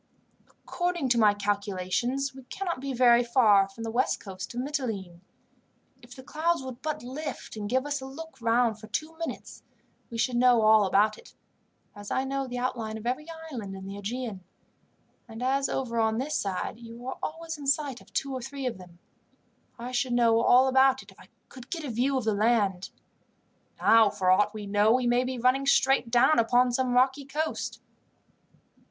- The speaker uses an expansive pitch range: No, average, 3.5 semitones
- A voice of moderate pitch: No, high, 245 Hz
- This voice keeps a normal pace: Yes, average, 195 wpm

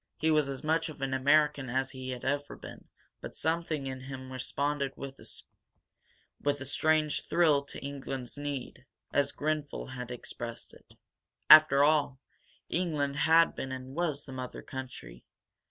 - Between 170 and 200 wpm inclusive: No, average, 150 wpm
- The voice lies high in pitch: No, medium, 140 Hz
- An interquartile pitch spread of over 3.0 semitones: No, narrow, 2.5 semitones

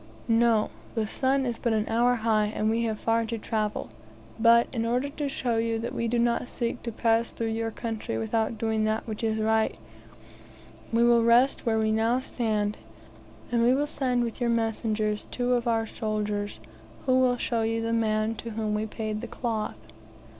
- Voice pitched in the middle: No, high, 225 Hz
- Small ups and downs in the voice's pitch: Yes, narrow, 1.5 semitones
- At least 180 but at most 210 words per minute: Yes, average, 190 wpm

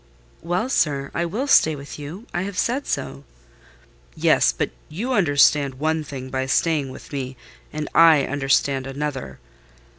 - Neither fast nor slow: Yes, average, 145 wpm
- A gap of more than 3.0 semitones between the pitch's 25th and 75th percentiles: Yes, average, 4.0 semitones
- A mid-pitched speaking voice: Yes, medium, 145 Hz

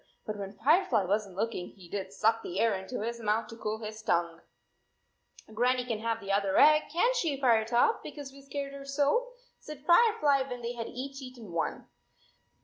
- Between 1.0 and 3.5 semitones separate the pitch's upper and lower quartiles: No, average, 4.8 semitones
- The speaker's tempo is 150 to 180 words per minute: No, average, 200 wpm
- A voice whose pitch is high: Yes, high, 235 Hz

